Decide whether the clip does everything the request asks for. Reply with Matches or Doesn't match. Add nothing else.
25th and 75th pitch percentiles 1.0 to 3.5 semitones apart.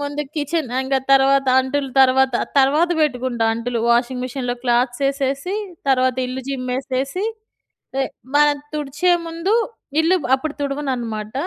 Matches